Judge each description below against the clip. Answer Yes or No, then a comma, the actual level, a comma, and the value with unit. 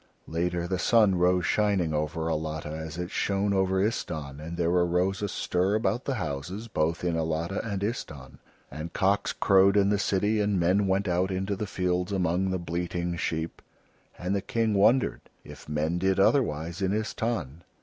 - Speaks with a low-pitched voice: Yes, very low, 90 Hz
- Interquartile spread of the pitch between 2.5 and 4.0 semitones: Yes, average, 3.2 semitones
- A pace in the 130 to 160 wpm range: No, average, 175 wpm